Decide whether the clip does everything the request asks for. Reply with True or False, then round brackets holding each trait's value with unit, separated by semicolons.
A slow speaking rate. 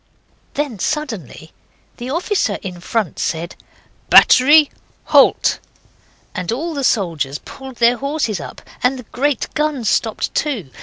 True (125 wpm)